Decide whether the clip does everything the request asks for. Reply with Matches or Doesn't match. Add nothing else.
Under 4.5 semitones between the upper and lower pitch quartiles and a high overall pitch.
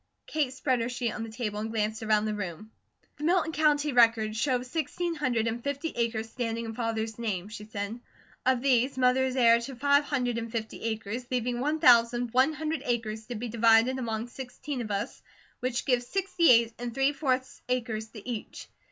Matches